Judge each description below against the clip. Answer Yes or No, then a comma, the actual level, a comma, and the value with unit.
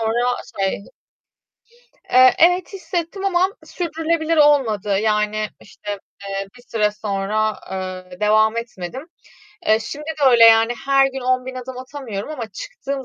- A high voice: Yes, high, 240 Hz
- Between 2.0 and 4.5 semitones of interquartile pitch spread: No, wide, 5.4 semitones